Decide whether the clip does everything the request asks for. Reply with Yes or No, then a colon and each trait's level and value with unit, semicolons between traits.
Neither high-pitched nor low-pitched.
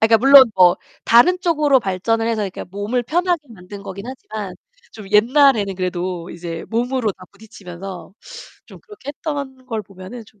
No: high, 220 Hz